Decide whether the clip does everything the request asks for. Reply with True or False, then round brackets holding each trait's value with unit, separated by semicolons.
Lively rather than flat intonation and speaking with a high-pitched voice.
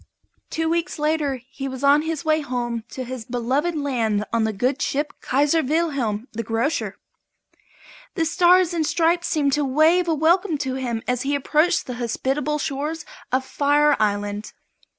False (4.2 semitones; 285 Hz)